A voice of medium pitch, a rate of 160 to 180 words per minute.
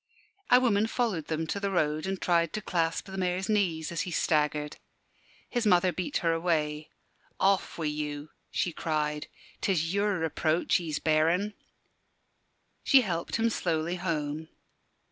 No: medium, 170 Hz; average, 145 wpm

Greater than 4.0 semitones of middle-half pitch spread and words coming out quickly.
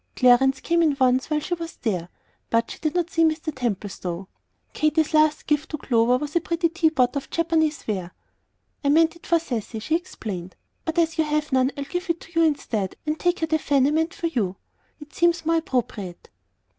Yes: average, 4.8 semitones; fast, 210 wpm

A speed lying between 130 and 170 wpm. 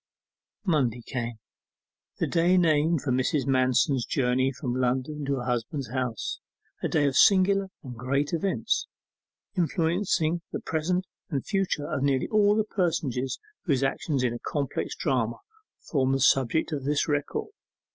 Yes: average, 145 wpm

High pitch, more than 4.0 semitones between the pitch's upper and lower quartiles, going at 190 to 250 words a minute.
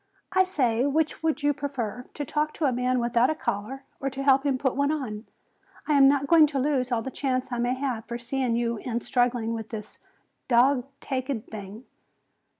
No: very high, 255 Hz; average, 3.0 semitones; fast, 205 wpm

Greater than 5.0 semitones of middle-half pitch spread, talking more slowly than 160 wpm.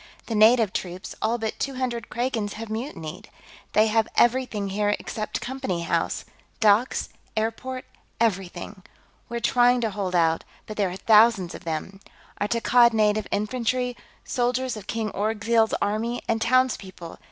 No: average, 2.9 semitones; average, 145 wpm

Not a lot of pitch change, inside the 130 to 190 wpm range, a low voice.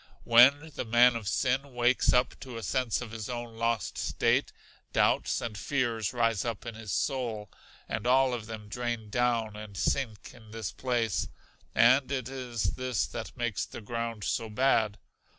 Yes: narrow, 2.2 semitones; average, 170 wpm; low, 115 Hz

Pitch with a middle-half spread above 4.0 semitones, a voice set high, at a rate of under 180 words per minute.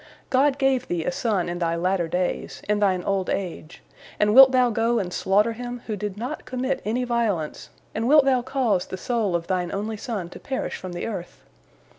No: average, 5.2 semitones; high, 210 Hz; fast, 205 wpm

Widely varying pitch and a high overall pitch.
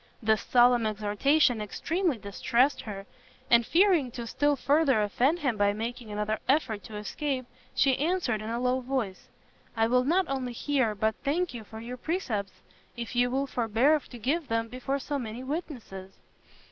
No: average, 4.3 semitones; high, 245 Hz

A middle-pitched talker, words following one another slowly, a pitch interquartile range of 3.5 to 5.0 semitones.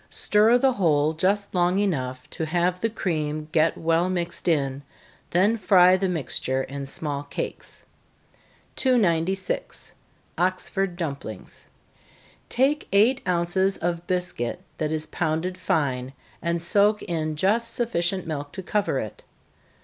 Yes: medium, 175 Hz; slow, 130 wpm; average, 3.9 semitones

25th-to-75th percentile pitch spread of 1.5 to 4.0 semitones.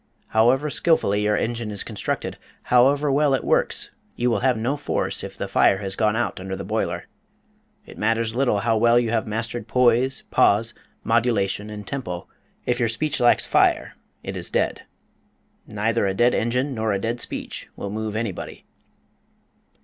Yes: average, 2.7 semitones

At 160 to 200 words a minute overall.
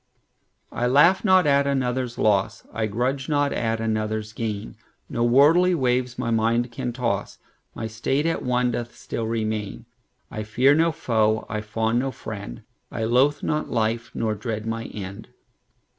No: average, 140 wpm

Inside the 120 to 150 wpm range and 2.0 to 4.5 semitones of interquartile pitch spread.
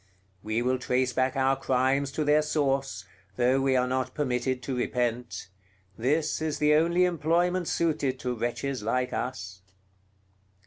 Yes: average, 145 wpm; average, 3.2 semitones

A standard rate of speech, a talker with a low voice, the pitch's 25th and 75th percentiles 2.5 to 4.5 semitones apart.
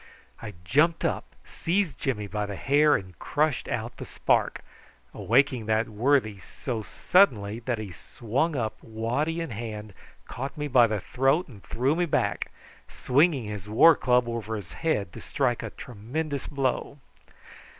No: average, 155 wpm; low, 125 Hz; average, 5.3 semitones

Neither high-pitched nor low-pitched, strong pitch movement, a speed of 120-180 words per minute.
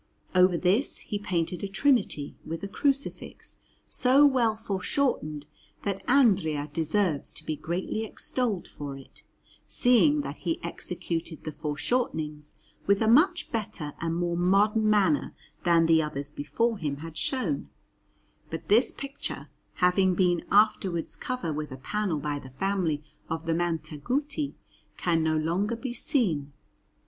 Yes: medium, 180 Hz; wide, 5.9 semitones; average, 140 wpm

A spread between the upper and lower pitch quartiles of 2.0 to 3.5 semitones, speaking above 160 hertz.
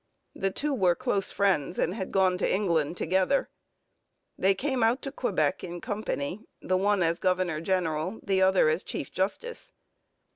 Yes: average, 3.0 semitones; high, 190 Hz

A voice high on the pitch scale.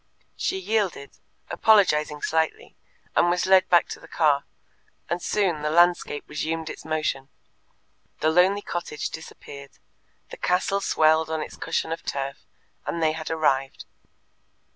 No: medium, 160 Hz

